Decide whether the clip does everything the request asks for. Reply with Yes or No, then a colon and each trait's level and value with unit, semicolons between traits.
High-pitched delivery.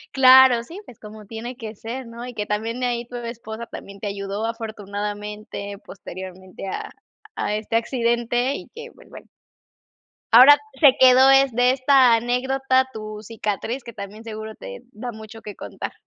Yes: high, 230 Hz